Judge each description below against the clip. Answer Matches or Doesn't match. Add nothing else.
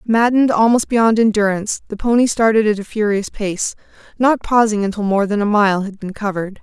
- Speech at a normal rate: Matches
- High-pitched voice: Matches